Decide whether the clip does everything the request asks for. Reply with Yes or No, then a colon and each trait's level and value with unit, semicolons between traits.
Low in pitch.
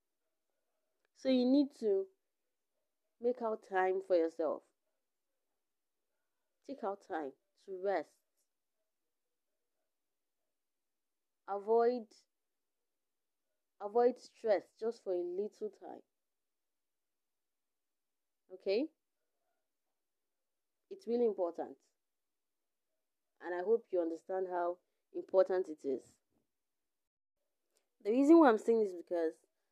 No: high, 220 Hz